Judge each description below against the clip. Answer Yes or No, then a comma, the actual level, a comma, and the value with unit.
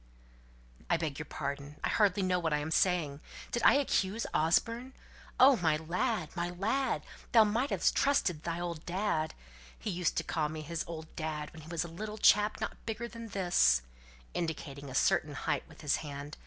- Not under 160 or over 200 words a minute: Yes, average, 185 wpm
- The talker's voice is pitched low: No, medium, 170 Hz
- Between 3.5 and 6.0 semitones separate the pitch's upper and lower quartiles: Yes, average, 5.2 semitones